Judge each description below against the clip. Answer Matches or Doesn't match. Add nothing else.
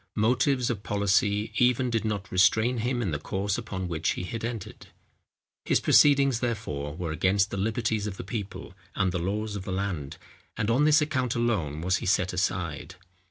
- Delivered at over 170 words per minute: Matches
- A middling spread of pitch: Matches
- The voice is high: Doesn't match